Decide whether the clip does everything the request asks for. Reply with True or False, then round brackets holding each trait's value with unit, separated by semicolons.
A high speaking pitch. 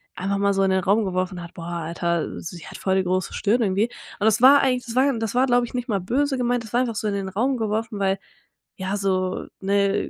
True (200 Hz)